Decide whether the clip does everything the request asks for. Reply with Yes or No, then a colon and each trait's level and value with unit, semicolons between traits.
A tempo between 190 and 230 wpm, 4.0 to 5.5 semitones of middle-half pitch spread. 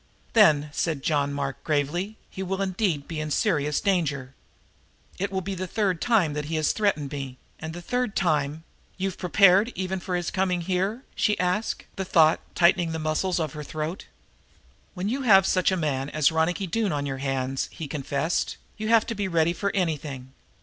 Yes: average, 195 wpm; average, 4.4 semitones